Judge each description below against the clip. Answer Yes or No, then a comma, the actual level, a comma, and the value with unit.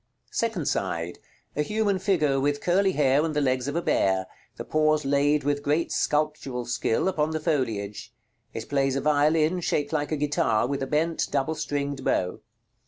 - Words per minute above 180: No, average, 175 wpm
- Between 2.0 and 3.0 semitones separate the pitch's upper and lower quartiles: Yes, narrow, 2.6 semitones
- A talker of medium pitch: Yes, medium, 145 Hz